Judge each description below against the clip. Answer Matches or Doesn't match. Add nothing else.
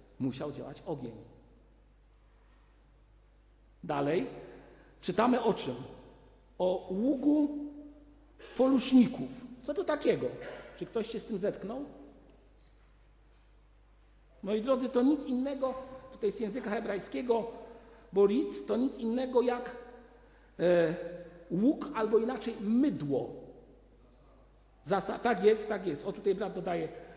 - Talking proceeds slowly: Matches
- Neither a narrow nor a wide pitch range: Doesn't match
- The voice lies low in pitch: Doesn't match